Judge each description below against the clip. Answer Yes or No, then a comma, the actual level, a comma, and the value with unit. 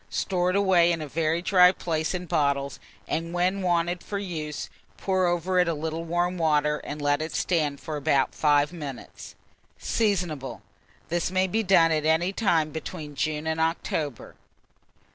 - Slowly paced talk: No, average, 165 wpm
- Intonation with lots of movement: No, average, 2.9 semitones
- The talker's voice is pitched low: No, medium, 165 Hz